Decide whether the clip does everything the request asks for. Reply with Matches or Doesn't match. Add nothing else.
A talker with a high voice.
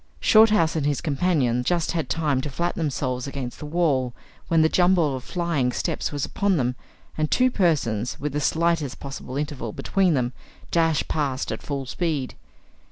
Doesn't match